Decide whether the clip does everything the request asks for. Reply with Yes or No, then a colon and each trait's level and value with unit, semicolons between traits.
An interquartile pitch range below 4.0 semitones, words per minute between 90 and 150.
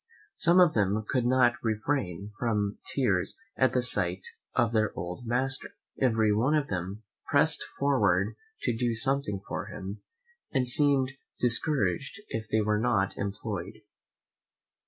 No: average, 4.5 semitones; slow, 135 wpm